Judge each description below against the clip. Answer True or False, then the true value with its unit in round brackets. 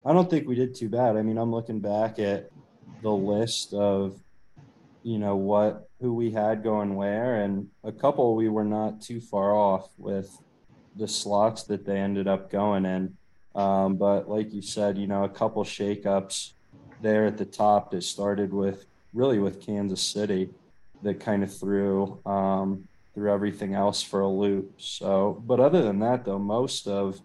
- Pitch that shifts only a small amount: True (1.6 semitones)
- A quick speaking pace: False (180 wpm)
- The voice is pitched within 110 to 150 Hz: False (100 Hz)